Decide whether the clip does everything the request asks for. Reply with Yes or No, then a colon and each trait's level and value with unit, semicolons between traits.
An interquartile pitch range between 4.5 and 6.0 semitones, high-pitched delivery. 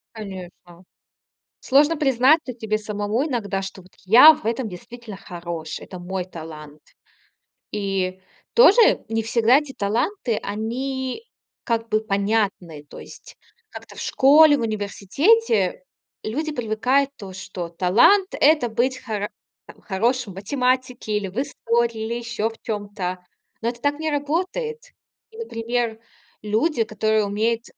Yes: average, 5.0 semitones; high, 225 Hz